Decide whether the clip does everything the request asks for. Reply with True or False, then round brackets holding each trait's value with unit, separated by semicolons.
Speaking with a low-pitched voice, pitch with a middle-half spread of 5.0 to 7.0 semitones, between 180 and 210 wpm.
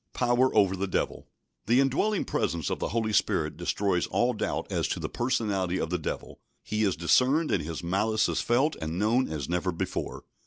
True (105 Hz; 5.5 semitones; 195 wpm)